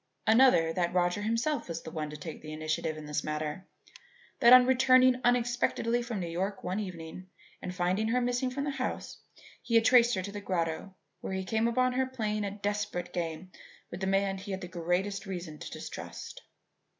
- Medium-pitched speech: No, high, 195 Hz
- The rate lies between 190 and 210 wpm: Yes, average, 200 wpm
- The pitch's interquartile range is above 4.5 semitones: Yes, wide, 5.4 semitones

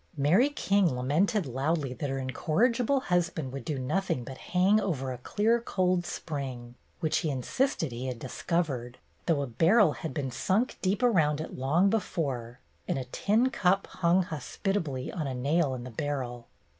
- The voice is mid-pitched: Yes, medium, 155 Hz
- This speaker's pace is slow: No, average, 170 wpm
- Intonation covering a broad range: Yes, wide, 6.4 semitones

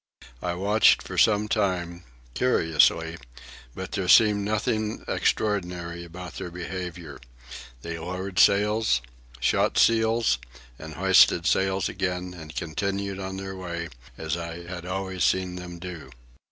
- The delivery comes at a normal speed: No, slow, 125 wpm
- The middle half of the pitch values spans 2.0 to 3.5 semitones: Yes, narrow, 2.4 semitones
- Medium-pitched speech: No, very low, 90 Hz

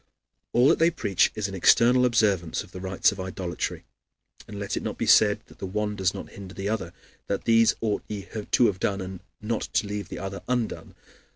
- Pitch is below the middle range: Yes, low, 100 Hz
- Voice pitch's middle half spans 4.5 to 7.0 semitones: No, average, 2.7 semitones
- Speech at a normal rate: No, fast, 215 wpm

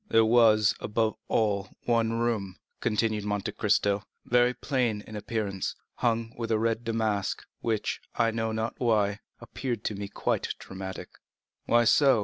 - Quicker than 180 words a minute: No, average, 140 wpm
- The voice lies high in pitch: No, low, 110 Hz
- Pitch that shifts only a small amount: Yes, narrow, 1.9 semitones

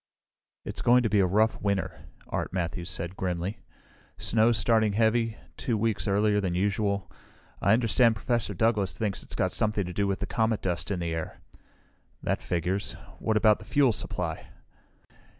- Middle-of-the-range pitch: No, low, 105 Hz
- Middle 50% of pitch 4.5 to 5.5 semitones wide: No, average, 3.0 semitones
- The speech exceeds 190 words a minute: No, average, 170 wpm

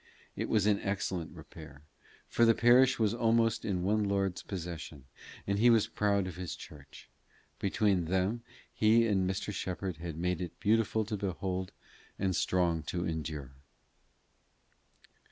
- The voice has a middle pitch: No, very low, 95 Hz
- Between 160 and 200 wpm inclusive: No, average, 150 wpm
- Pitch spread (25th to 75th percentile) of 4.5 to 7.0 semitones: No, average, 3.6 semitones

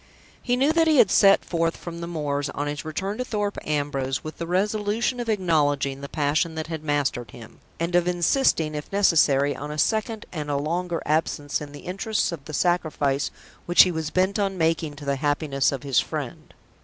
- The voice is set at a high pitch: No, medium, 160 Hz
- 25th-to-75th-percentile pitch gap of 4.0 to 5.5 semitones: Yes, average, 4.6 semitones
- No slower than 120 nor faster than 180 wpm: No, fast, 205 wpm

